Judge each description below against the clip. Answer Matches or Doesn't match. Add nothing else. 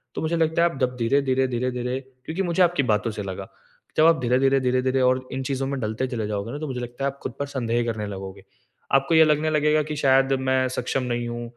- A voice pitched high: Doesn't match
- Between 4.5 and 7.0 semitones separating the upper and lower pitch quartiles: Doesn't match